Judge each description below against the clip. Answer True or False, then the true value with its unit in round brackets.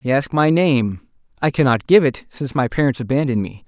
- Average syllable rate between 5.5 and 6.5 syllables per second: True (5.9 syllables/s)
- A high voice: False (135 Hz)